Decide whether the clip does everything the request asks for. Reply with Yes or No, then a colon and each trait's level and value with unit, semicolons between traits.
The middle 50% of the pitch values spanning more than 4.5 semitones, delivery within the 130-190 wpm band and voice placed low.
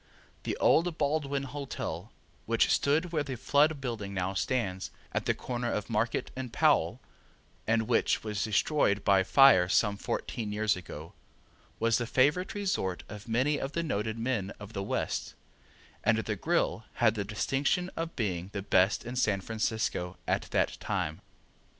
Yes: wide, 5.4 semitones; average, 160 wpm; low, 115 Hz